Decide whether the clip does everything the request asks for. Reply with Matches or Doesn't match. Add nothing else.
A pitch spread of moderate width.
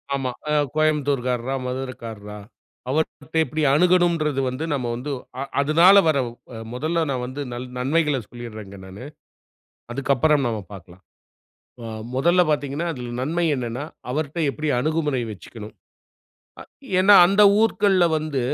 Matches